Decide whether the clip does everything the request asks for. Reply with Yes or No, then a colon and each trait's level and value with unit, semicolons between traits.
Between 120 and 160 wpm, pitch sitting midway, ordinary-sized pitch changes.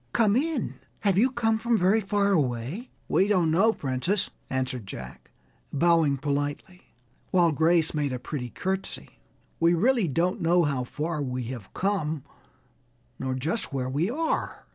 No: average, 150 wpm; medium, 165 Hz; wide, 6.8 semitones